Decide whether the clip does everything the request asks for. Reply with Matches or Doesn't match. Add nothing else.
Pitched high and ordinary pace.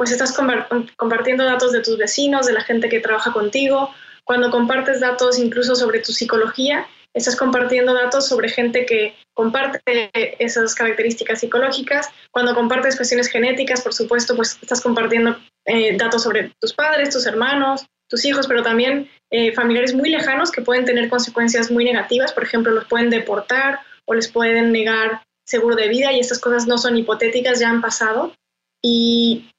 Matches